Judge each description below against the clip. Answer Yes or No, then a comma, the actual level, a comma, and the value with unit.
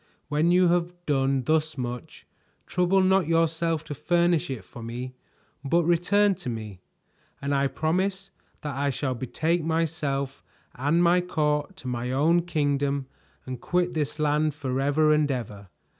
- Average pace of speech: Yes, average, 150 wpm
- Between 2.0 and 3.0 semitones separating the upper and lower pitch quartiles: No, average, 4.1 semitones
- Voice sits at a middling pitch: Yes, medium, 150 Hz